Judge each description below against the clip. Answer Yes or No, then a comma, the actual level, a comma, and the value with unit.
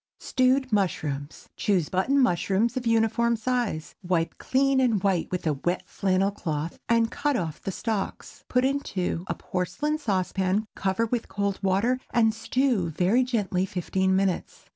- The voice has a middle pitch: No, high, 200 Hz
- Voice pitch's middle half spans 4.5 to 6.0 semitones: Yes, average, 4.8 semitones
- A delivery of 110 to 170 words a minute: Yes, average, 150 wpm